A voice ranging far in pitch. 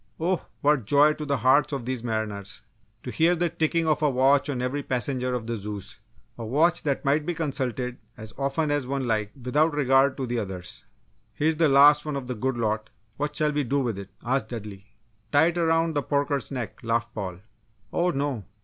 No: average, 4.2 semitones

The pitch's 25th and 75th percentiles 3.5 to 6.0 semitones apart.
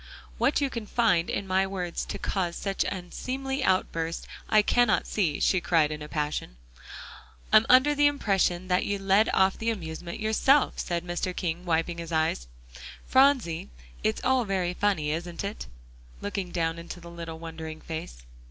Yes: average, 4.4 semitones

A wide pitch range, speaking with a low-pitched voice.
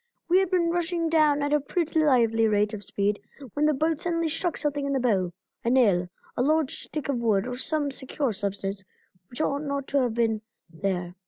No: wide, 6.3 semitones; very high, 275 Hz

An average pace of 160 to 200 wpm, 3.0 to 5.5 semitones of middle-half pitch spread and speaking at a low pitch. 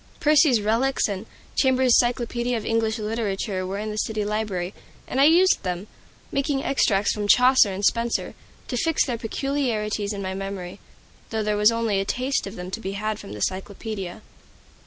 No: average, 180 wpm; average, 3.8 semitones; high, 215 Hz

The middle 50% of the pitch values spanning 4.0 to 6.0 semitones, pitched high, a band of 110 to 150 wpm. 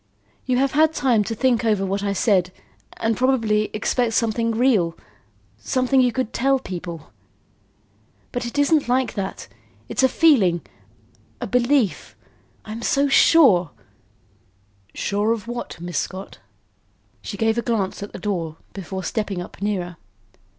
Yes: average, 5.0 semitones; high, 220 Hz; average, 145 wpm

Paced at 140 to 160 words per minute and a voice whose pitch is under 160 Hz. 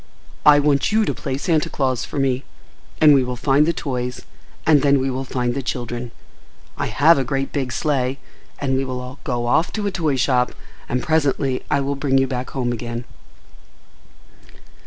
No: average, 185 wpm; low, 135 Hz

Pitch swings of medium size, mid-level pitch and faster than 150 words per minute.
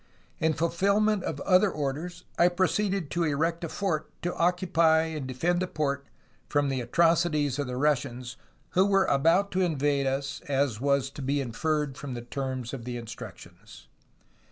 Yes: average, 4.2 semitones; medium, 150 Hz; average, 165 wpm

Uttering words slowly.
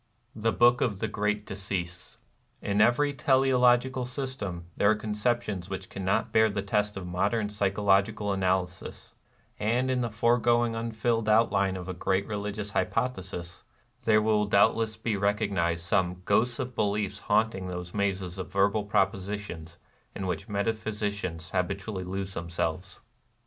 No: average, 145 wpm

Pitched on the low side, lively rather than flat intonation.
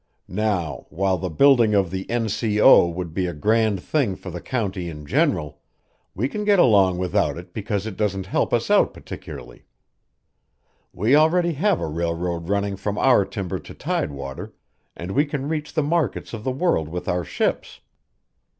Yes: low, 100 Hz; wide, 6.3 semitones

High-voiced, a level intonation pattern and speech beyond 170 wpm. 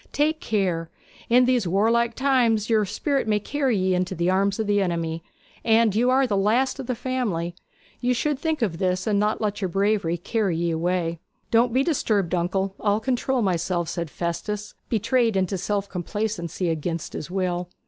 No: high, 205 Hz; average, 4.8 semitones; average, 180 wpm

